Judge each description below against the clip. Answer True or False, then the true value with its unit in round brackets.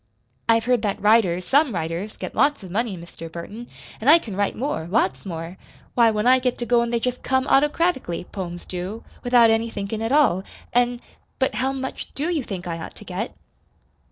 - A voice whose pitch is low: False (225 Hz)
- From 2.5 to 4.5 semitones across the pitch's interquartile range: False (5.1 semitones)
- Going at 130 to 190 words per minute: False (200 wpm)